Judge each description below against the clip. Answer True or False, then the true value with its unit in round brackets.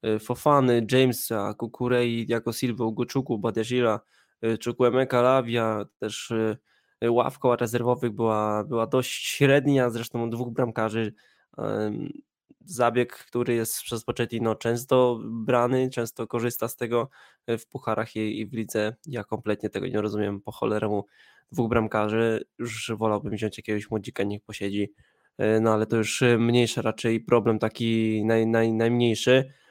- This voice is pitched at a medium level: False (115 Hz)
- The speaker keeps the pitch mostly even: True (1.9 semitones)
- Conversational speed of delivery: True (130 wpm)